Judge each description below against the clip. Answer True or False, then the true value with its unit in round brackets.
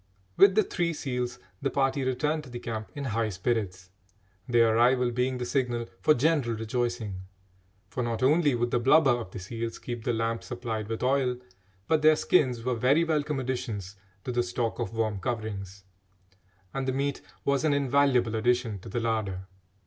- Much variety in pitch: False (3.1 semitones)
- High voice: False (120 Hz)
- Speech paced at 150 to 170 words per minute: False (180 wpm)